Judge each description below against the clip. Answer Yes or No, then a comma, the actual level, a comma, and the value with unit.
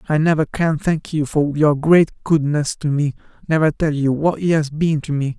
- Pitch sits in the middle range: Yes, medium, 150 Hz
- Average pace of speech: No, fast, 225 wpm